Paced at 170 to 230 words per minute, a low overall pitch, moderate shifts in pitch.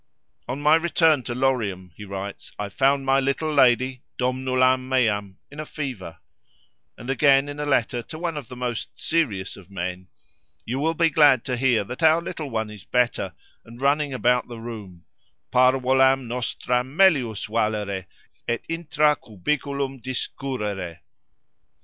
No: average, 145 wpm; low, 130 Hz; average, 4.6 semitones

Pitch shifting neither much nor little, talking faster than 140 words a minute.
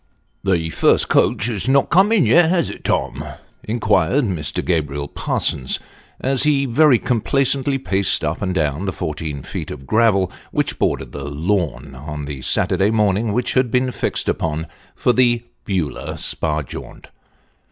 No: wide, 8.6 semitones; average, 165 wpm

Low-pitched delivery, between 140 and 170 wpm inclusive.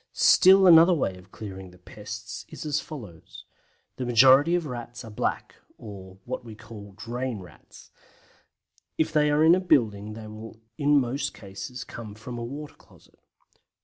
Yes: low, 115 Hz; average, 165 wpm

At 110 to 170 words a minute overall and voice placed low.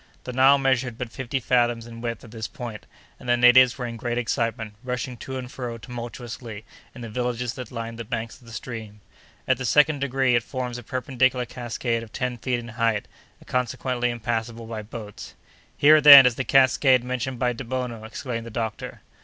No: average, 195 wpm; low, 120 Hz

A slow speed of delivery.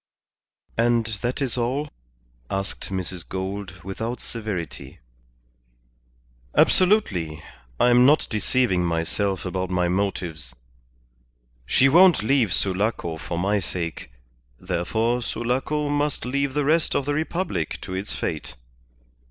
Yes: slow, 115 wpm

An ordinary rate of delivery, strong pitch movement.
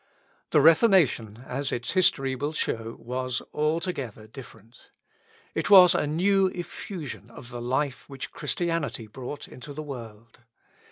No: slow, 130 wpm; wide, 5.7 semitones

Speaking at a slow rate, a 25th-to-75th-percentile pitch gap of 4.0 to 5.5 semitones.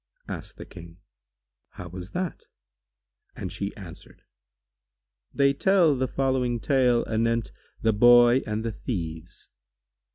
Yes: slow, 120 wpm; average, 5.0 semitones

